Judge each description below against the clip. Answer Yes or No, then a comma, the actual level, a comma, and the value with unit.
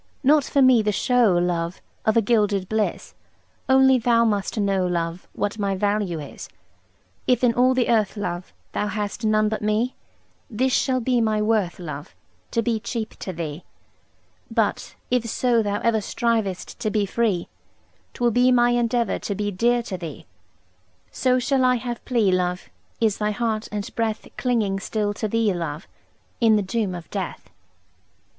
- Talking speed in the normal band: Yes, average, 165 wpm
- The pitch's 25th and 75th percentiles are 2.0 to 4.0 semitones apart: Yes, average, 3.6 semitones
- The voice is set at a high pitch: Yes, high, 215 Hz